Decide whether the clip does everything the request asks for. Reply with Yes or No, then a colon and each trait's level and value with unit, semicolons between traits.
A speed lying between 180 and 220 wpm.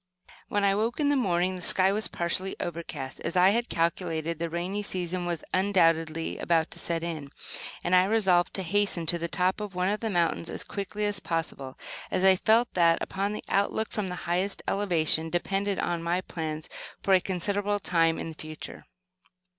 Yes: average, 190 wpm